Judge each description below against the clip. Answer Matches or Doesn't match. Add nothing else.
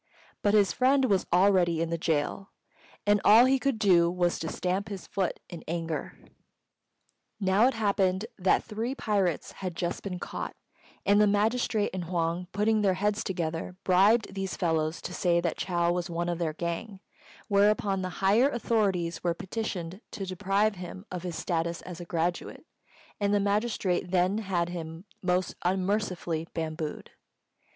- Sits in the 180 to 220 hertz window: Matches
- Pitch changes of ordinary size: Matches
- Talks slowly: Doesn't match